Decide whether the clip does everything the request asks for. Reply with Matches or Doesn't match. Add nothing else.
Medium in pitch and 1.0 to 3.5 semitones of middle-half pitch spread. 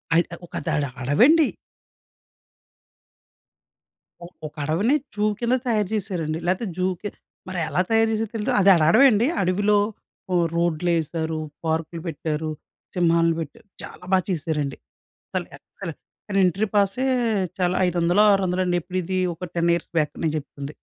Doesn't match